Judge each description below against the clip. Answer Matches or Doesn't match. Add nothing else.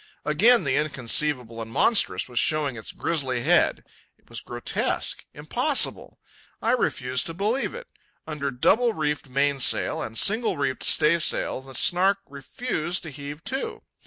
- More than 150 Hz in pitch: Doesn't match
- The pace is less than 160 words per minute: Matches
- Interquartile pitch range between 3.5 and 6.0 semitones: Matches